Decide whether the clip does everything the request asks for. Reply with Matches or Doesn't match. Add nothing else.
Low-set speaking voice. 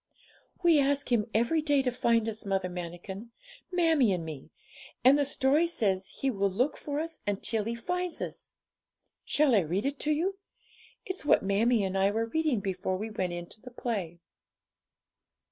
Doesn't match